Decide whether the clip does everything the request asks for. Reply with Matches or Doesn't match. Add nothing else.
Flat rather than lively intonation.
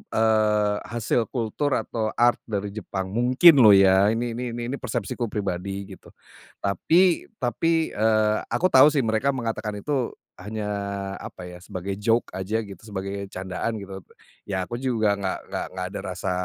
Doesn't match